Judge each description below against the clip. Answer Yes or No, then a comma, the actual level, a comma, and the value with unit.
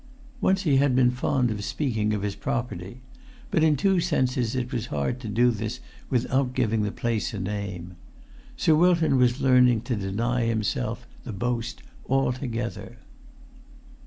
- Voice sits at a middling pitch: No, low, 120 Hz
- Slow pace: No, average, 155 wpm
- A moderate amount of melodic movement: Yes, average, 3.4 semitones